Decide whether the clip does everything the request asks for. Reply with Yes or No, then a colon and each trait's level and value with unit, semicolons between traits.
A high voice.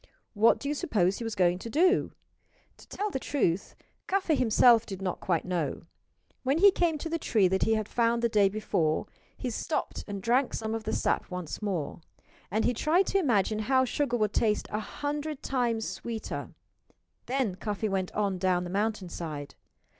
Yes: high, 220 Hz